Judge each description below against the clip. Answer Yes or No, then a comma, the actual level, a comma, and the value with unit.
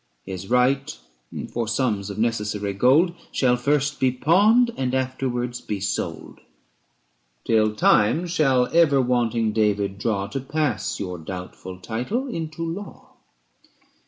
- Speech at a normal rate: No, slow, 130 wpm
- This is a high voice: No, low, 125 Hz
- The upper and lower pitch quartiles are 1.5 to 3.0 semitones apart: No, wide, 5.6 semitones